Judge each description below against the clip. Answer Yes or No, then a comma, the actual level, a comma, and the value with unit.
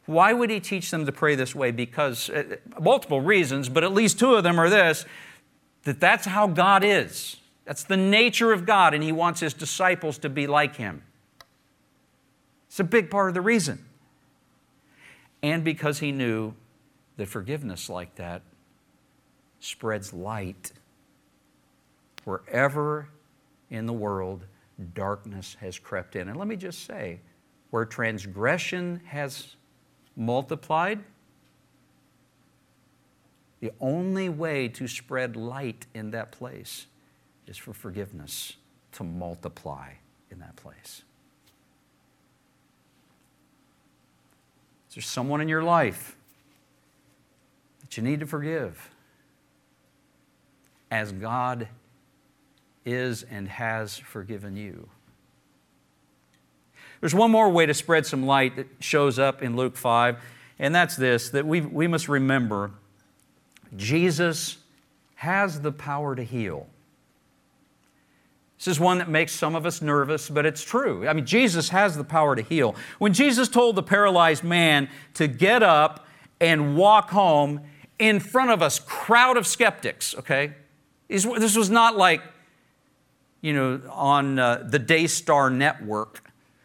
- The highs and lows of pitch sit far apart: Yes, wide, 6.4 semitones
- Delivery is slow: Yes, slow, 130 wpm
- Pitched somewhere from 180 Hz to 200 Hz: No, medium, 145 Hz